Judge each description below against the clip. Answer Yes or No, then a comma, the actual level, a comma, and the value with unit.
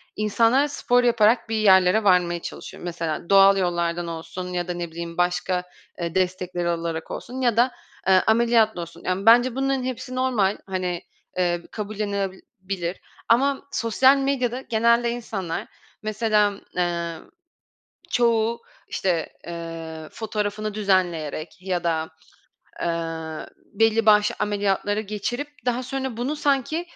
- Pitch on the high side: Yes, high, 200 Hz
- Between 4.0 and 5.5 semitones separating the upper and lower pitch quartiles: Yes, average, 5.1 semitones